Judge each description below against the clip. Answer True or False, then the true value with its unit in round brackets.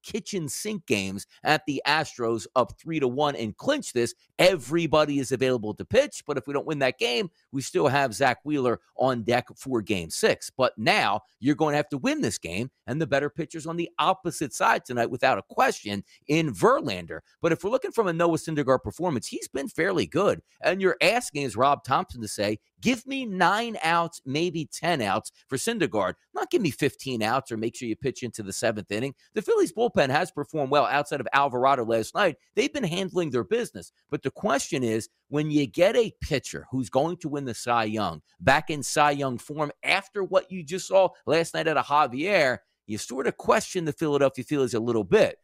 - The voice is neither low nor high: True (145 Hz)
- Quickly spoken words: True (215 wpm)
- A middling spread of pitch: False (5.7 semitones)